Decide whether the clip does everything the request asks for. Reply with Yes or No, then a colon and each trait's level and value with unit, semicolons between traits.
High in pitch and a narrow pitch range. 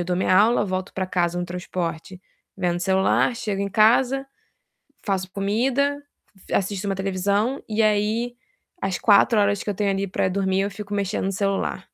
Yes: high, 200 Hz; narrow, 2.3 semitones